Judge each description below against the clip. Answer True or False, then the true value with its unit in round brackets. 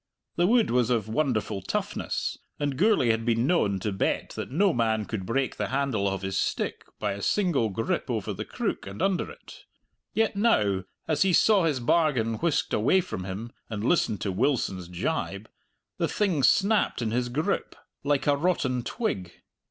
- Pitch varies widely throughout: True (7.9 semitones)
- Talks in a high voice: False (125 Hz)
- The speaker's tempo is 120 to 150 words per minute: False (180 wpm)